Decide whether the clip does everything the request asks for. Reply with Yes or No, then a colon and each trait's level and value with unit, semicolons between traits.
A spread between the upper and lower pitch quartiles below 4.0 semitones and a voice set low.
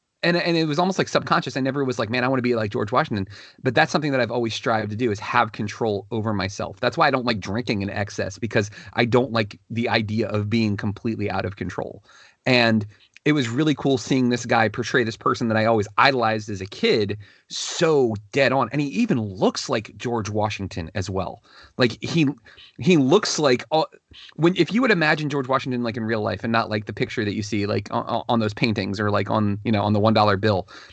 Yes: average, 3.6 semitones; low, 115 Hz